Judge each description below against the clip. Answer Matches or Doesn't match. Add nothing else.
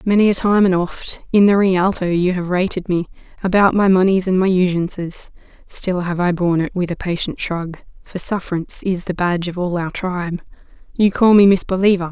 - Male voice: Doesn't match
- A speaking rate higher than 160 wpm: Matches